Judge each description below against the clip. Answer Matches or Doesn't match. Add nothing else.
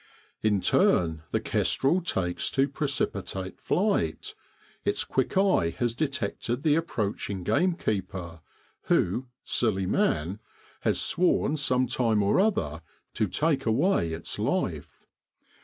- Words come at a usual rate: Doesn't match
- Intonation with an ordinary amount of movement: Doesn't match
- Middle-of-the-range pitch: Doesn't match